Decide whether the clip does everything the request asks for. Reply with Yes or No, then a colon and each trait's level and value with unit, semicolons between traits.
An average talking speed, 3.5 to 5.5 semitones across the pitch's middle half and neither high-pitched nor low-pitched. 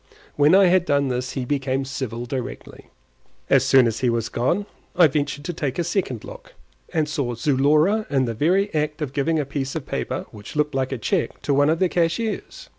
No: fast, 210 wpm; average, 3.8 semitones; medium, 145 Hz